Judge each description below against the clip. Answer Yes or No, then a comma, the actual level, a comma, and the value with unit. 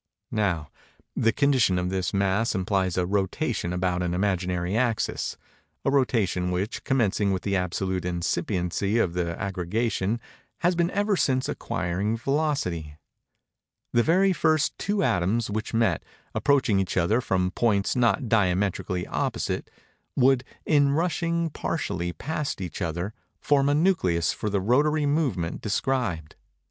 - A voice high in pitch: No, low, 105 Hz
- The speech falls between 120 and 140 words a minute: Yes, slow, 135 wpm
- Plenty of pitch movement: Yes, wide, 7.0 semitones